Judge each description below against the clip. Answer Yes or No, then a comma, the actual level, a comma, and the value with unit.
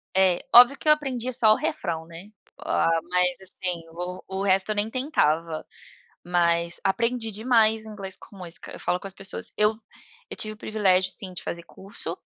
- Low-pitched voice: No, high, 195 Hz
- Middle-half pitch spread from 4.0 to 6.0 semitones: No, average, 3.6 semitones